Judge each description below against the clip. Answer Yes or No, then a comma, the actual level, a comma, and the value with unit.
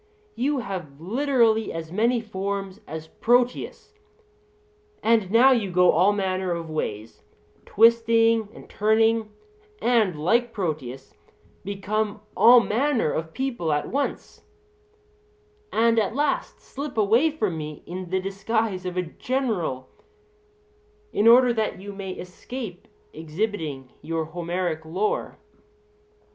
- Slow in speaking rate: Yes, slow, 120 wpm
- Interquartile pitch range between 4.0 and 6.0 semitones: Yes, average, 5.0 semitones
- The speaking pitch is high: Yes, high, 200 Hz